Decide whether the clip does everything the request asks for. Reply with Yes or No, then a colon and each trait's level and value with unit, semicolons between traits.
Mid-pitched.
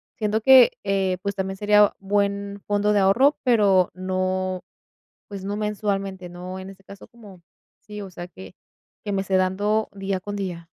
No: high, 195 Hz